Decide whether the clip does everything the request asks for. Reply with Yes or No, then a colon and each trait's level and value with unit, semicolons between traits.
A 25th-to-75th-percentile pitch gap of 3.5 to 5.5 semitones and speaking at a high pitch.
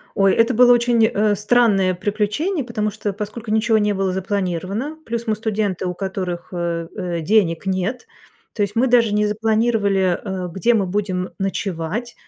No: average, 3.1 semitones; high, 210 Hz